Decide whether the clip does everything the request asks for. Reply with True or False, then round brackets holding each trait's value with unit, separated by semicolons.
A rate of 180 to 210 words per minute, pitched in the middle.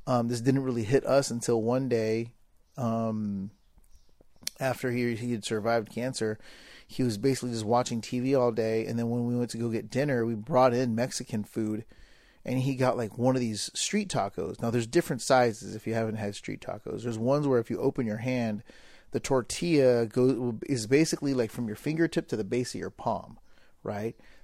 False (200 wpm; 120 Hz)